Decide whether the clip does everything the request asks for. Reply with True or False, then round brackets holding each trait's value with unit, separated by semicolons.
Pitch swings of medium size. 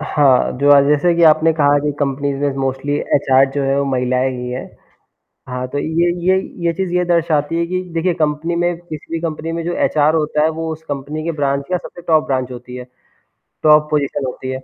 True (3.1 semitones)